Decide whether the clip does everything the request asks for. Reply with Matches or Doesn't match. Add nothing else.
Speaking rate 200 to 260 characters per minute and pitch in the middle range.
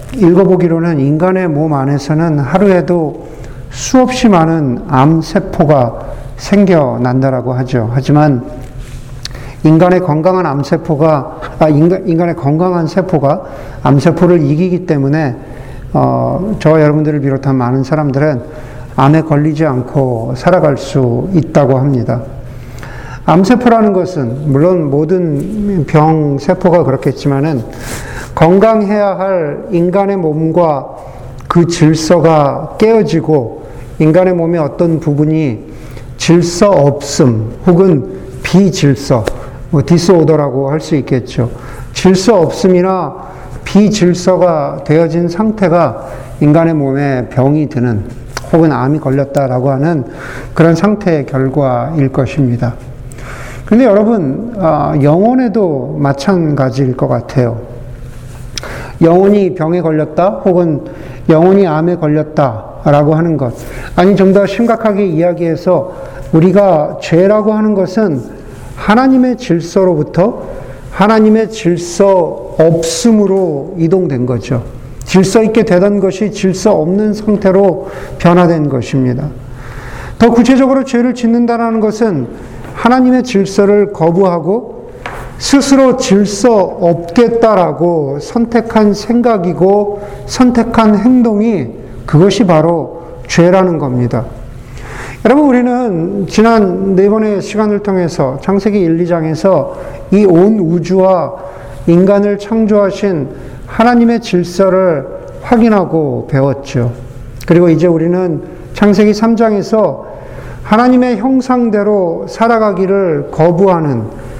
Matches